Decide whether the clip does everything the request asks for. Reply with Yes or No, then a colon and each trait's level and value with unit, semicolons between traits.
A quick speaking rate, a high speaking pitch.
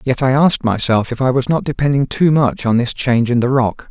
No: fast, 260 wpm; low, 130 Hz